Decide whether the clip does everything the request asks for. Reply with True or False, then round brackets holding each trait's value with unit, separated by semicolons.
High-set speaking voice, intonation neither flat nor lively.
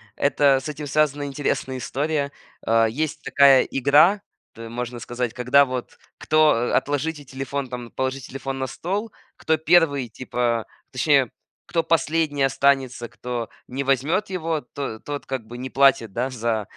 False (135 Hz; 3.2 semitones)